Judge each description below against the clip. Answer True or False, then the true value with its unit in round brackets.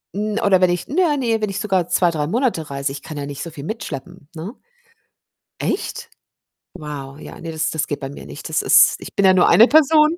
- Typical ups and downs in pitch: False (7.3 semitones)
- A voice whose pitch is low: False (180 Hz)